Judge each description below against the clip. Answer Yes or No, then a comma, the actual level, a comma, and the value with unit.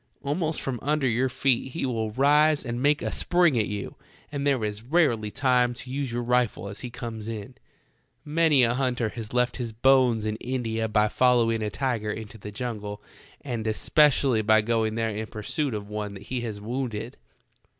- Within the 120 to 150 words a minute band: No, average, 190 wpm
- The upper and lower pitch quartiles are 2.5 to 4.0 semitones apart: Yes, average, 3.4 semitones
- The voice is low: Yes, low, 120 Hz